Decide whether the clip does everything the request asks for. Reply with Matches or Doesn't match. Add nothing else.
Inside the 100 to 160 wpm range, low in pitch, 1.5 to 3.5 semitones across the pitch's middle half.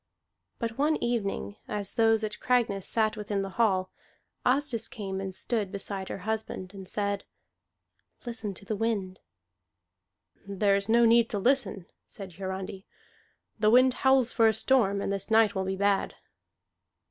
Doesn't match